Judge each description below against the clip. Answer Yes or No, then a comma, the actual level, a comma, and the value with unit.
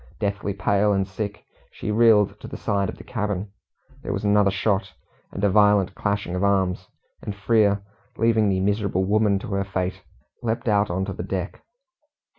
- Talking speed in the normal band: Yes, average, 180 wpm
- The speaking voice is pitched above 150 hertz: No, low, 100 Hz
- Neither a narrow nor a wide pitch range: No, narrow, 1.4 semitones